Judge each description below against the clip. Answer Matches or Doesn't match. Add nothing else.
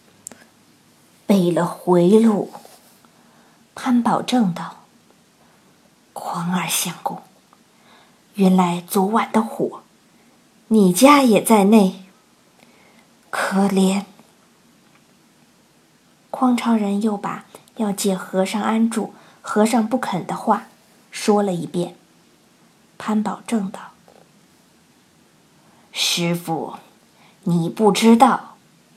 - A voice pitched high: Matches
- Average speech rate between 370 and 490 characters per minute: Doesn't match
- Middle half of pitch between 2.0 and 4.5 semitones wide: Matches